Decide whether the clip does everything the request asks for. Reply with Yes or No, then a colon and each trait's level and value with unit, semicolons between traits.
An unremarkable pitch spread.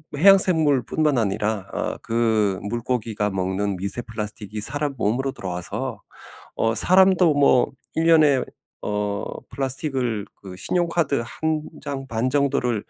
No: wide, 5.8 semitones